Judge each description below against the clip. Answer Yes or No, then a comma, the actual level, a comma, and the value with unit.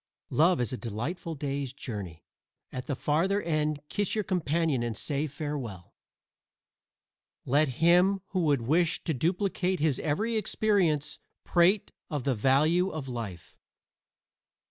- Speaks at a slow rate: Yes, slow, 130 wpm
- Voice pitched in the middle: Yes, medium, 150 Hz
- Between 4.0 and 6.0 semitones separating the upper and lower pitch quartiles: Yes, average, 5.2 semitones